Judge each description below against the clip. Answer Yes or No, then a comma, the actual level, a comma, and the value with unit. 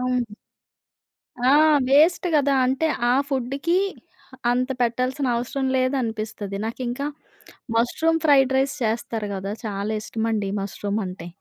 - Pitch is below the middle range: No, high, 245 Hz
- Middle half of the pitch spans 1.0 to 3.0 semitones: No, average, 3.7 semitones